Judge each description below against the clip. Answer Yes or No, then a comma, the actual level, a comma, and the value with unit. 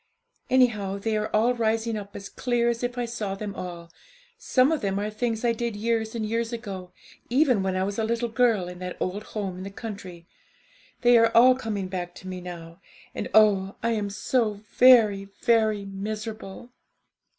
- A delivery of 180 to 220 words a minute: Yes, average, 190 wpm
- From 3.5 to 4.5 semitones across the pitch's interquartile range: No, average, 3.1 semitones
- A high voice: Yes, high, 215 Hz